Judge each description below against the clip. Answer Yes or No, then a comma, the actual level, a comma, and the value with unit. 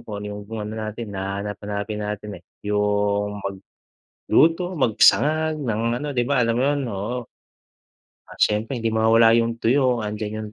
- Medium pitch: No, low, 110 Hz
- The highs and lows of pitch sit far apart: No, average, 2.9 semitones